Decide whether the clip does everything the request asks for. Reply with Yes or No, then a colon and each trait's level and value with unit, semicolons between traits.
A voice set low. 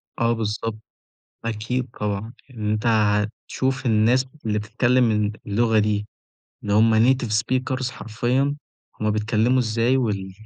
Yes: low, 110 Hz